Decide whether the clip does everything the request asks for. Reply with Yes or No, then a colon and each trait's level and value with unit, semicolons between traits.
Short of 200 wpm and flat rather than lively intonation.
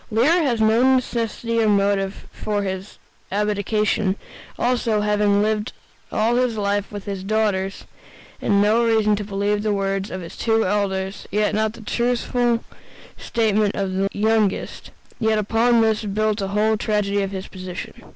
Yes: average, 160 wpm; narrow, 1.8 semitones